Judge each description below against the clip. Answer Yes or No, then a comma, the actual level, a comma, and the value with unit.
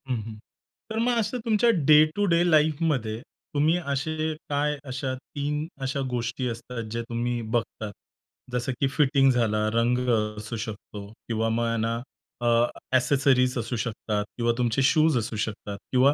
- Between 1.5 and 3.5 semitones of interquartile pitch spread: No, average, 4.2 semitones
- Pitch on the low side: Yes, low, 125 Hz